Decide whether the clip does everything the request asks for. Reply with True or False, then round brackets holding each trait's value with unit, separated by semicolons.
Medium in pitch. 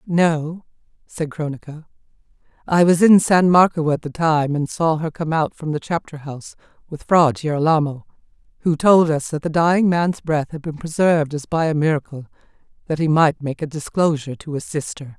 True (155 Hz)